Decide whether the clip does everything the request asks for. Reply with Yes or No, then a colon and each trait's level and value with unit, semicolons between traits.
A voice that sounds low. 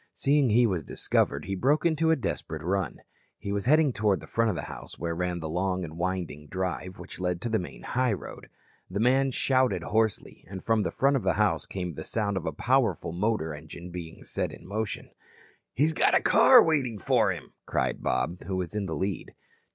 Yes: low, 100 Hz